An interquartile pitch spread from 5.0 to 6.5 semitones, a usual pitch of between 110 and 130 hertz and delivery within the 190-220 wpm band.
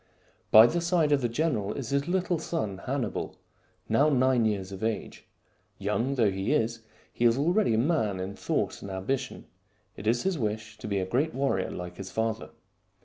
Yes: wide, 5.6 semitones; low, 115 Hz; average, 195 wpm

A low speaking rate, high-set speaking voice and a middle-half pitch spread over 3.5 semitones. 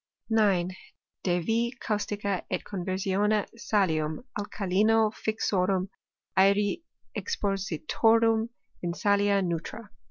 No: slow, 90 wpm; high, 200 Hz; average, 2.7 semitones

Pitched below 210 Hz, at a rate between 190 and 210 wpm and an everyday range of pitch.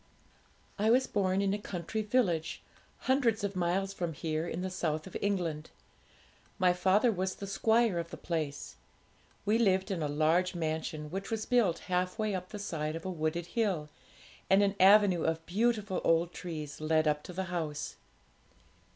No: medium, 185 Hz; average, 175 wpm; average, 3.9 semitones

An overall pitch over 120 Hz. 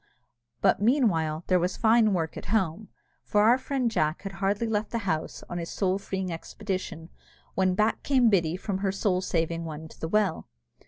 Yes: high, 190 Hz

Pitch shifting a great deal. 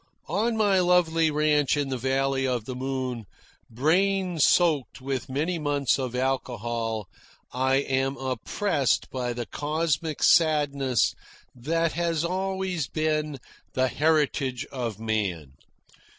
No: average, 4.1 semitones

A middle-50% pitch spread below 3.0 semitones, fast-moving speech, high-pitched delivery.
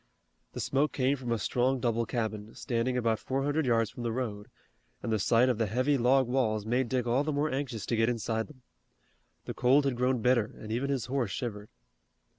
No: narrow, 2.6 semitones; fast, 215 wpm; low, 125 Hz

